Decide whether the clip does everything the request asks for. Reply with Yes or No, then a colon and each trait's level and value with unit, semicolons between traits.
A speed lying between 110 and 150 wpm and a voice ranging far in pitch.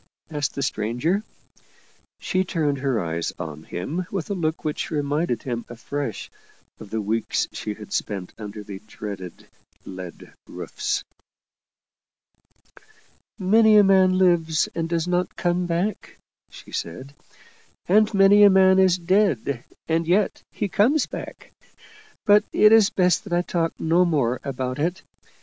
Yes: average, 145 wpm; wide, 7.9 semitones